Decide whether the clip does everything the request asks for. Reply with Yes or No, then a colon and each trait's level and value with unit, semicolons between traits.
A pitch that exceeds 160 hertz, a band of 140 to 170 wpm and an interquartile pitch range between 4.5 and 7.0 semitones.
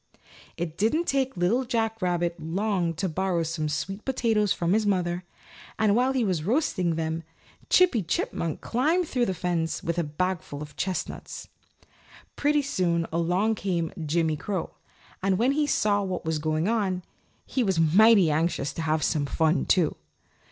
Yes: medium, 185 Hz; average, 160 wpm; average, 5.1 semitones